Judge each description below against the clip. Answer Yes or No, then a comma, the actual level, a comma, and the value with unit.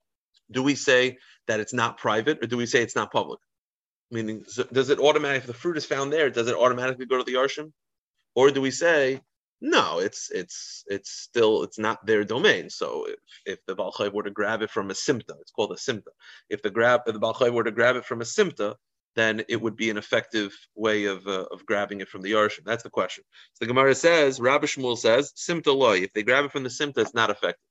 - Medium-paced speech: No, fast, 235 wpm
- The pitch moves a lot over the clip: No, average, 4.3 semitones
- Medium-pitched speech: No, low, 125 Hz